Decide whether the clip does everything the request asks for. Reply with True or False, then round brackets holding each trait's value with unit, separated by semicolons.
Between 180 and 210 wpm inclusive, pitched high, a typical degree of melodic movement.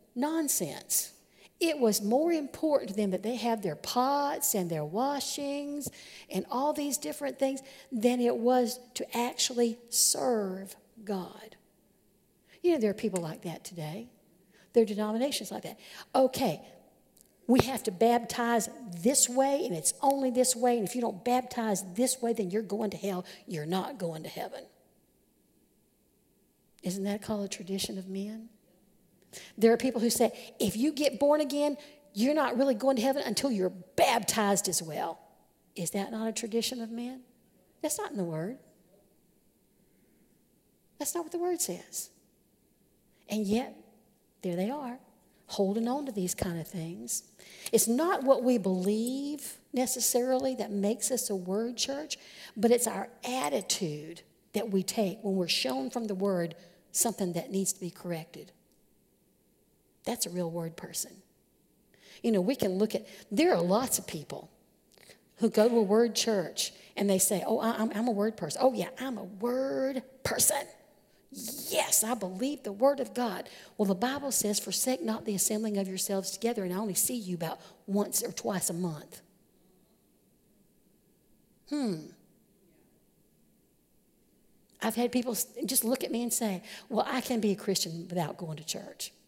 False (165 wpm; 225 Hz; 4.7 semitones)